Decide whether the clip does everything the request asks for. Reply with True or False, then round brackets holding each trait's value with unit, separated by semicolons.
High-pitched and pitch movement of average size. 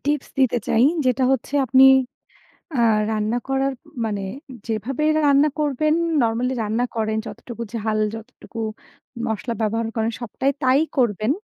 True (240 Hz; 3.3 semitones)